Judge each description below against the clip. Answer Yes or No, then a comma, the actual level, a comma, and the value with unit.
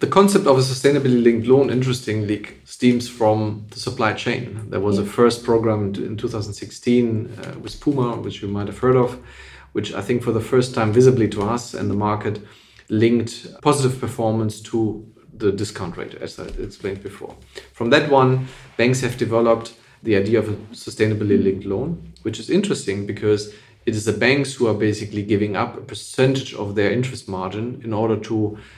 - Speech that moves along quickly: No, average, 180 wpm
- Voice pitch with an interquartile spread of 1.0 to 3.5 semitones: Yes, average, 3.1 semitones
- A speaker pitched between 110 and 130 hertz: Yes, low, 115 Hz